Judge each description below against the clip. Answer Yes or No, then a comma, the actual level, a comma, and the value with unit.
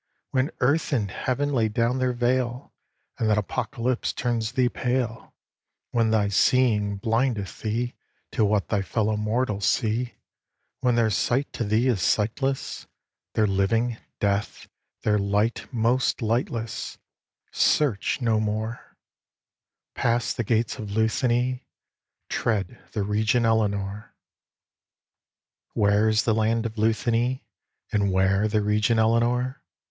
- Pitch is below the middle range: Yes, low, 115 Hz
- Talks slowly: Yes, slow, 125 wpm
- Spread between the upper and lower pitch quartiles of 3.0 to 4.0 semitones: No, narrow, 2.6 semitones